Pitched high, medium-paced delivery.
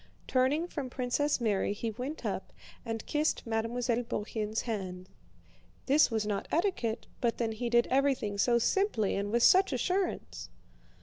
Yes: high, 235 Hz; average, 145 wpm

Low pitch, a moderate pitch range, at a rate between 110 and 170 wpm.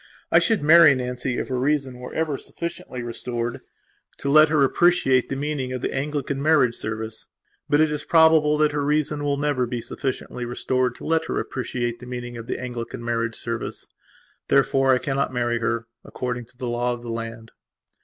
No: low, 130 Hz; average, 3.5 semitones; average, 190 wpm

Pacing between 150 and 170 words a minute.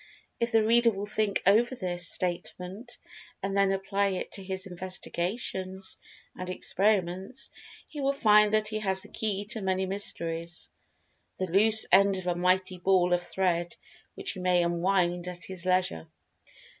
Yes: average, 155 wpm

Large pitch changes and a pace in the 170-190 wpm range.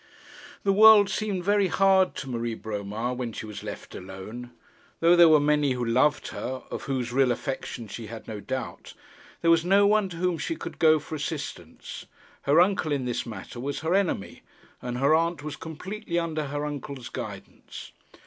Yes: wide, 6.0 semitones; average, 185 wpm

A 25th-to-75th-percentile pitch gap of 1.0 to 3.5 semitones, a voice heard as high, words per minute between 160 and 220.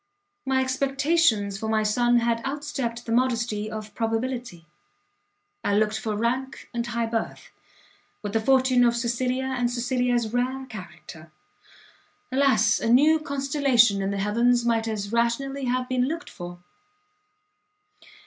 No: average, 3.0 semitones; high, 240 Hz; slow, 135 wpm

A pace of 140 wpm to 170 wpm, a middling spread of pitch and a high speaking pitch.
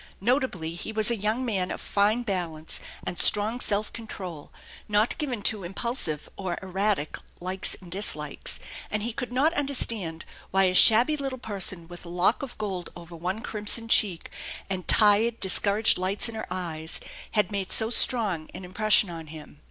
Yes: average, 165 wpm; average, 4.0 semitones; high, 200 Hz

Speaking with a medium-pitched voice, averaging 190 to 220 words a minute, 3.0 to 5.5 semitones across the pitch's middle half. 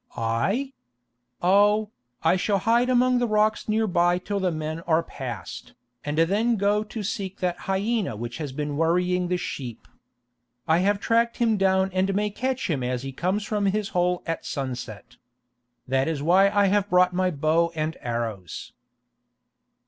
No: medium, 180 Hz; average, 165 wpm; average, 5.0 semitones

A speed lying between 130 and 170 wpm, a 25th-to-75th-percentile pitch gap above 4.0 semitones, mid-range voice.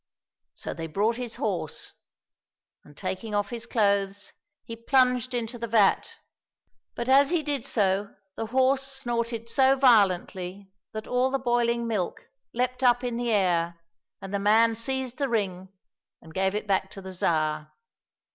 No: average, 160 wpm; average, 4.4 semitones; high, 225 Hz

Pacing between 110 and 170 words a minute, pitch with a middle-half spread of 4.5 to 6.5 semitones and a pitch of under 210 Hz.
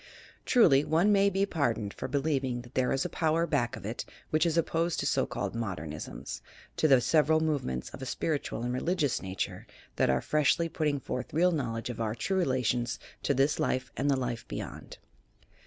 No: average, 195 wpm; average, 4.9 semitones; low, 135 Hz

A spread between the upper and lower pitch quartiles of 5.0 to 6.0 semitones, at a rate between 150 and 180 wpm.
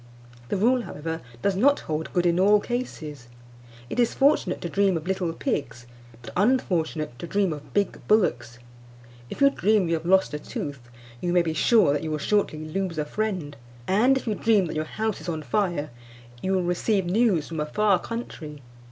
No: average, 5.3 semitones; average, 195 wpm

